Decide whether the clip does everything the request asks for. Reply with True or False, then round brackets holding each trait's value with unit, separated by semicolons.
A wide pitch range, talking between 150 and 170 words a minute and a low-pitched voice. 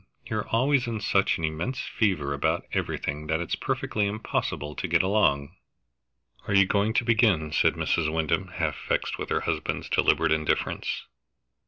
True (5.7 semitones; 160 wpm; 95 Hz)